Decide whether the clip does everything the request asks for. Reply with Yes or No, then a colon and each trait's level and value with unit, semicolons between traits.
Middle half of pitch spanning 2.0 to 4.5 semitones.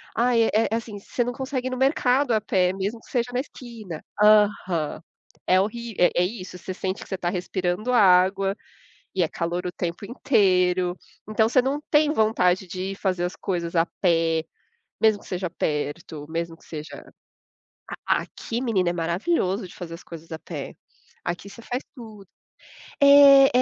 No: average, 4.9 semitones